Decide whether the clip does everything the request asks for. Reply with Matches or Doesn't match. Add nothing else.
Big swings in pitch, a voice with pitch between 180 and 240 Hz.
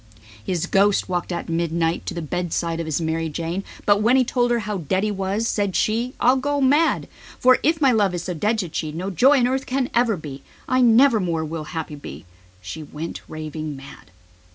Matches